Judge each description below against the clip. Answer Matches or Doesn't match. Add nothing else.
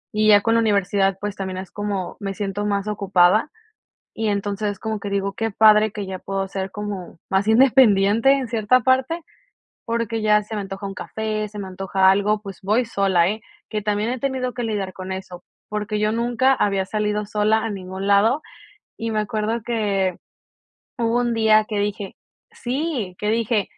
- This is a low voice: Doesn't match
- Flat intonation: Matches